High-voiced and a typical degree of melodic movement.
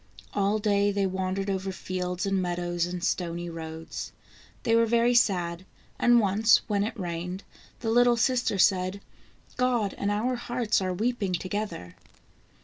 Yes: high, 195 Hz; average, 3.8 semitones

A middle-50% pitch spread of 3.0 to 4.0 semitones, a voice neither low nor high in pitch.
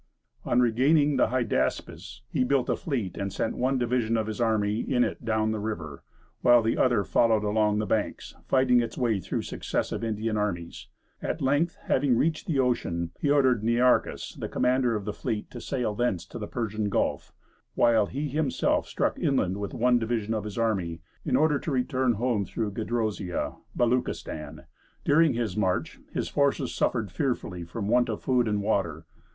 No: average, 3.4 semitones; low, 115 Hz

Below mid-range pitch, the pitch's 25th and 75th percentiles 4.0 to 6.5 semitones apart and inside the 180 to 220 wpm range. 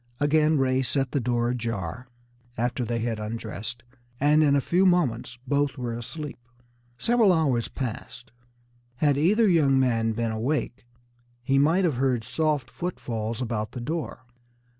No: low, 130 Hz; average, 4.3 semitones; average, 145 wpm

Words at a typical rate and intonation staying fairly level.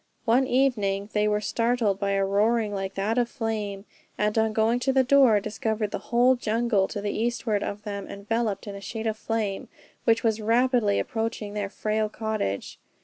Yes: average, 180 wpm; narrow, 2.3 semitones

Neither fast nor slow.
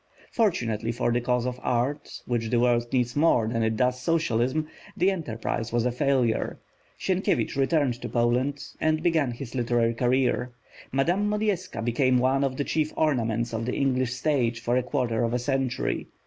Yes: average, 175 wpm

